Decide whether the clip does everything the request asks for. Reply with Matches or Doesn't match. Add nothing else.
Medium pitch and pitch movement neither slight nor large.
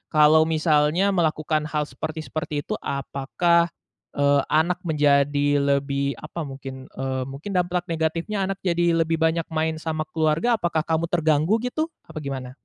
Matches